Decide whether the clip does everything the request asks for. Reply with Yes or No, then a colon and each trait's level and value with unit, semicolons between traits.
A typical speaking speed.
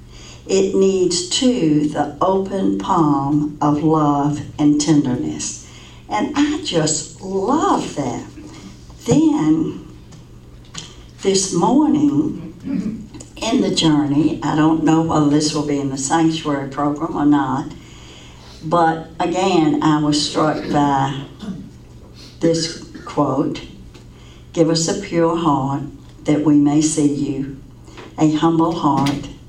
No: slow, 110 wpm